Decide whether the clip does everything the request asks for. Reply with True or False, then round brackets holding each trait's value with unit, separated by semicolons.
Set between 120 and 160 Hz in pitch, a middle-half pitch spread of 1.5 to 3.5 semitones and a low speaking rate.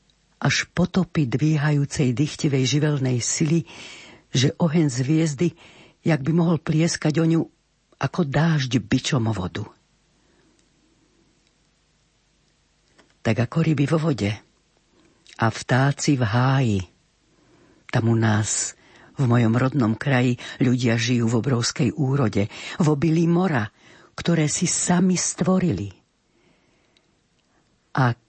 False (140 Hz; 5.3 semitones; 105 wpm)